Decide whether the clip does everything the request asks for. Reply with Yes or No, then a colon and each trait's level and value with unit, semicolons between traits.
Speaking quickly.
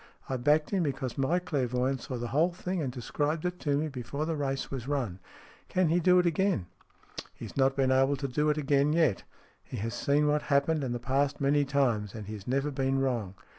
Yes: fast, 235 wpm